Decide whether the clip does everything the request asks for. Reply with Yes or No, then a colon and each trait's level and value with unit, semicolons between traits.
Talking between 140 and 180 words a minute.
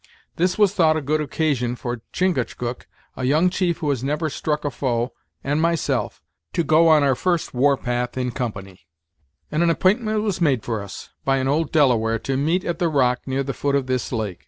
No: fast, 205 wpm